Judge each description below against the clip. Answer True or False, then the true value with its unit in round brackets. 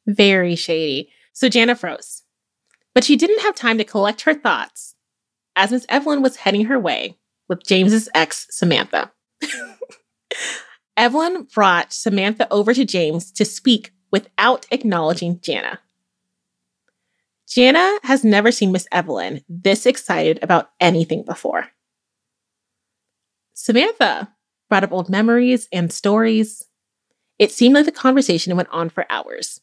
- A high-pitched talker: True (215 Hz)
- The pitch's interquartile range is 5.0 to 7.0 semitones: True (5.6 semitones)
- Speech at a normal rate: False (130 wpm)